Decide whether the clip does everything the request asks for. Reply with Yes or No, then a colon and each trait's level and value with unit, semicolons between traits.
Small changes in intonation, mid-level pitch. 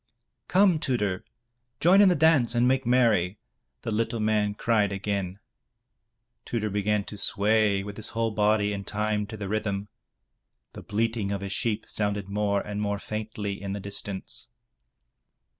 No: narrow, 2.1 semitones; low, 105 Hz